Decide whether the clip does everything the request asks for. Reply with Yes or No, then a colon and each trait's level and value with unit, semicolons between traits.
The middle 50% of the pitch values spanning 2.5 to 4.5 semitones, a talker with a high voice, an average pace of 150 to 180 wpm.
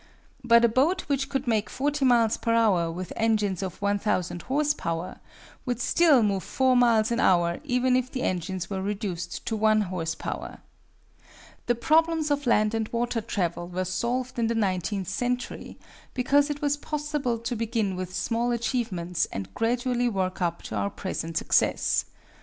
No: average, 5.2 semitones; high, 230 Hz; average, 170 wpm